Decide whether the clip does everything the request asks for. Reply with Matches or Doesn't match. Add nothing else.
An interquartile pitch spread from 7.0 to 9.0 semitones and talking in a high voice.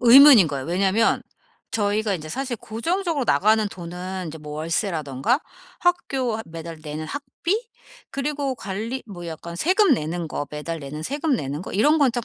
Matches